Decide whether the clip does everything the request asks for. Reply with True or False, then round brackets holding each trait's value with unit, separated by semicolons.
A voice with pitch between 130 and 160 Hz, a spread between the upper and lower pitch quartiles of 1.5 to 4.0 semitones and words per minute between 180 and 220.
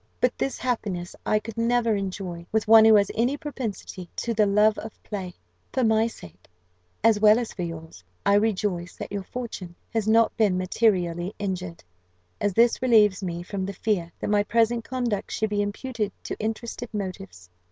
False (210 Hz; 3.5 semitones; 185 wpm)